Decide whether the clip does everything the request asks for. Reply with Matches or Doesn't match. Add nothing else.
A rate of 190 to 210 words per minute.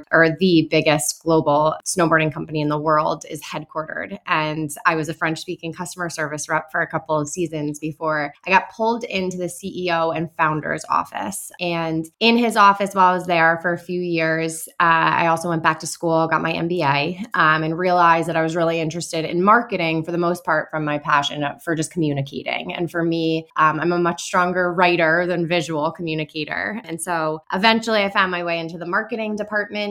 Matches